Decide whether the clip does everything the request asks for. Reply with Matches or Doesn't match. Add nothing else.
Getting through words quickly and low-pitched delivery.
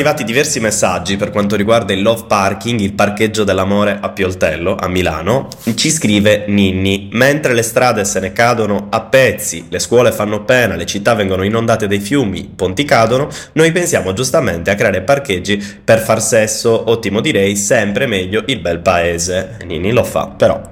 Matches